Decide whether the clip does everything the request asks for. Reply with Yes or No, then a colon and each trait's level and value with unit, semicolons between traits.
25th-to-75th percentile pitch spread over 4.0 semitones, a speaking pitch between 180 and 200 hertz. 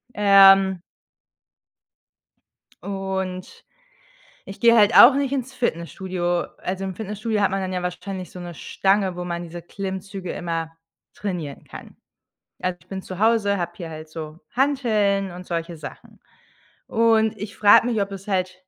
No: average, 2.8 semitones; high, 190 Hz